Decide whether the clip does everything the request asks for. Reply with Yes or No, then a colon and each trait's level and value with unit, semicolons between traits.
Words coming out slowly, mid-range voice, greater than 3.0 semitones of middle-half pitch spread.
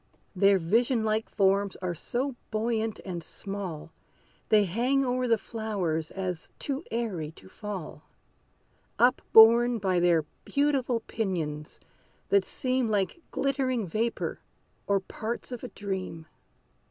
No: slow, 125 wpm; high, 215 Hz; average, 4.4 semitones